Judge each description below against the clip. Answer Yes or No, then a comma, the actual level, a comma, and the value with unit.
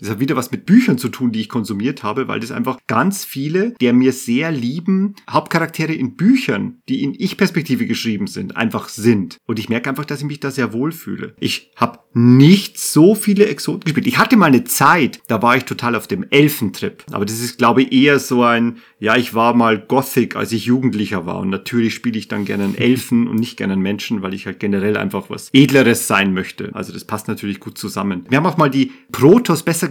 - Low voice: Yes, low, 125 Hz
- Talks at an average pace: No, fast, 225 wpm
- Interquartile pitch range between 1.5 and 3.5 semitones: No, average, 5.3 semitones